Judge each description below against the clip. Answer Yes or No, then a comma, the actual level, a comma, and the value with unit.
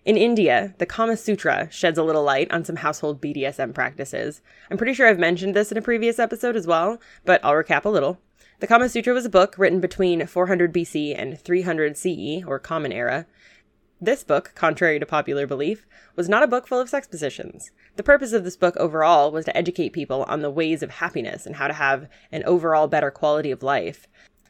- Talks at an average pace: No, fast, 210 wpm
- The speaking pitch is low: No, medium, 175 Hz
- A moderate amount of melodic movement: No, wide, 5.7 semitones